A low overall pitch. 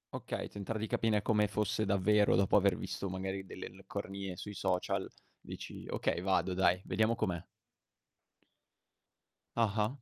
Yes: low, 100 Hz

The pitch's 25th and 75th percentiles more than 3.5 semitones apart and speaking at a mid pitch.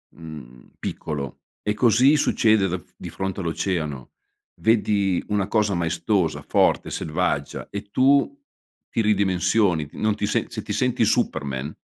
No: average, 5.1 semitones; very low, 95 Hz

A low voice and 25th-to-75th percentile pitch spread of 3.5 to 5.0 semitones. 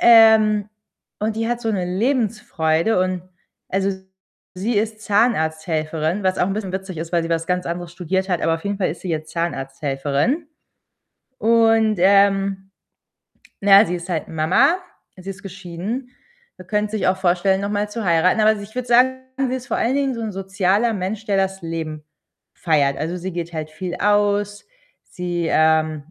No: high, 190 Hz; average, 4.1 semitones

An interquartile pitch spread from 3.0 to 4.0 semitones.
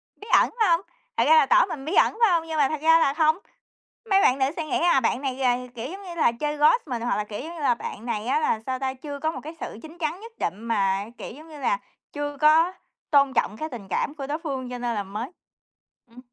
No: average, 4.7 semitones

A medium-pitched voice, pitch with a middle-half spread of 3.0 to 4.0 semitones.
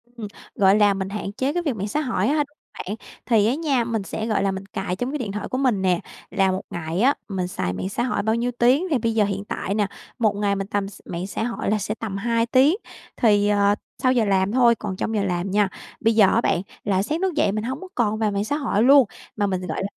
No: high, 210 Hz; average, 3.7 semitones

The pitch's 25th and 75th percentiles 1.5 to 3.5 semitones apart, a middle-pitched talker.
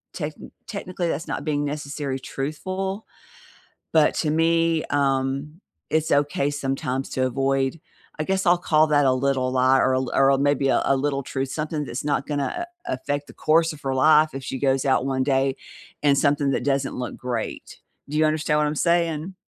Yes: narrow, 2.5 semitones; medium, 145 Hz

